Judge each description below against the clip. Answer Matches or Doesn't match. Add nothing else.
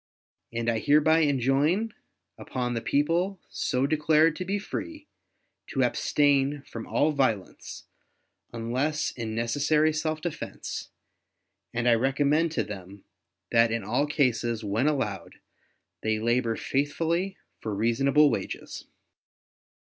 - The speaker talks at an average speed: Doesn't match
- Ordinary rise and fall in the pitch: Matches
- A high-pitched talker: Doesn't match